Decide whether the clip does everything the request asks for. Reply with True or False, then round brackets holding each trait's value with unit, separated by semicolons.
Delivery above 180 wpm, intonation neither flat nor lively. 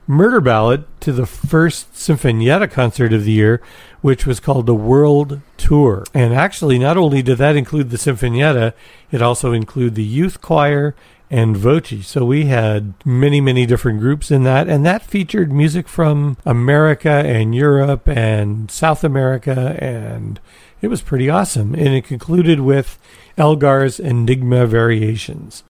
False (150 wpm; 3.6 semitones)